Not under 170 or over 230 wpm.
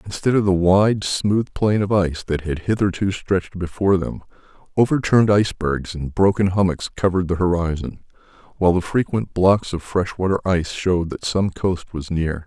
Yes: average, 175 wpm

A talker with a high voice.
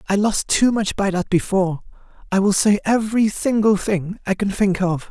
Yes: high, 200 Hz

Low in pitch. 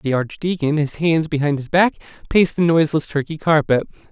No: medium, 155 Hz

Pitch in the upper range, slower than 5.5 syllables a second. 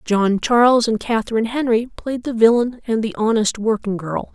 Yes: high, 225 Hz; 5.2 syllables/s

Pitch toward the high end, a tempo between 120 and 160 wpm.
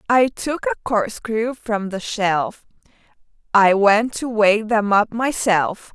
Yes: high, 220 Hz; average, 140 wpm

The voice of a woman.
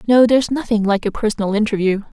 Yes: female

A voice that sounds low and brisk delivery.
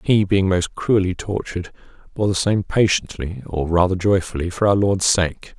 No: very low, 95 Hz; average, 170 wpm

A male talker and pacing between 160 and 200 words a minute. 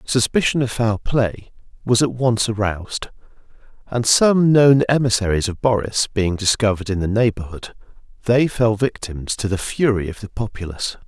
No: male; average, 150 wpm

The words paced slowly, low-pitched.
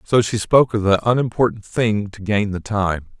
No: fast, 205 wpm; low, 105 Hz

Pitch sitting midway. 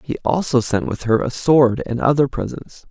No: low, 130 Hz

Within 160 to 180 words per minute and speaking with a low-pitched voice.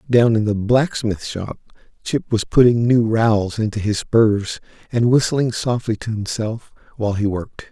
Yes: average, 165 wpm; low, 110 Hz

